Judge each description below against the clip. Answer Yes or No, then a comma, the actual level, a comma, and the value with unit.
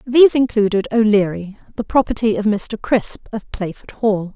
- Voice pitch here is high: Yes, high, 215 Hz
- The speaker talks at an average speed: Yes, average, 150 wpm